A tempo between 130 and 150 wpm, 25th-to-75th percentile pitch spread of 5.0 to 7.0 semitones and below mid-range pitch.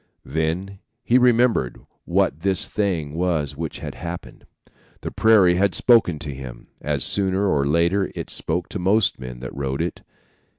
No: average, 160 wpm; average, 5.3 semitones; very low, 85 Hz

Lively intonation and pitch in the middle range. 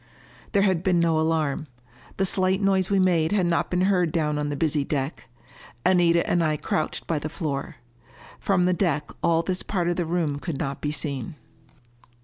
No: average, 3.4 semitones; medium, 170 Hz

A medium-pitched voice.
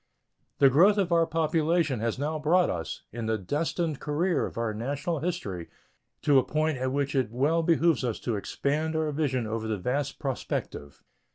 Yes: medium, 145 Hz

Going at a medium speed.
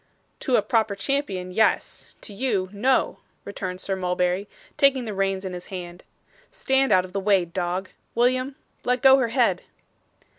Yes: average, 160 wpm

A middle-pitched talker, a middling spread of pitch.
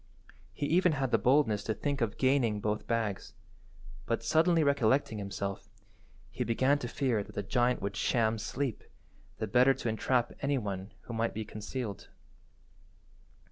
No: low, 115 Hz; average, 4.2 semitones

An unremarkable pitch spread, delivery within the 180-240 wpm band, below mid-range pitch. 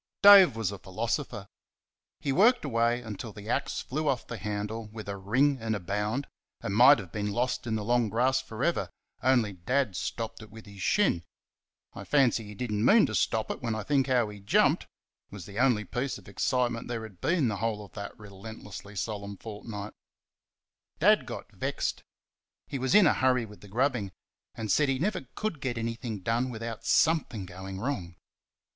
Yes: average, 3.9 semitones; average, 195 wpm; low, 115 Hz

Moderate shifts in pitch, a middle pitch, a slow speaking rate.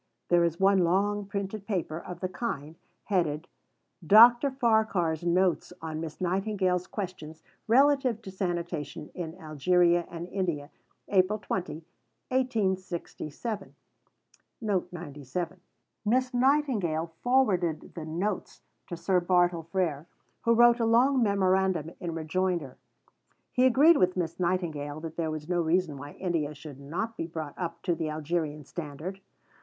Yes: average, 4.1 semitones; medium, 180 Hz; slow, 130 wpm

